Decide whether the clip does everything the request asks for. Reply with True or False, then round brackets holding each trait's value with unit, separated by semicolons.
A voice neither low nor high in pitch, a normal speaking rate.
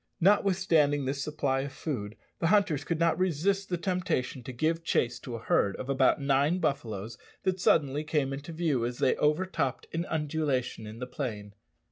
True (145 Hz; 175 wpm)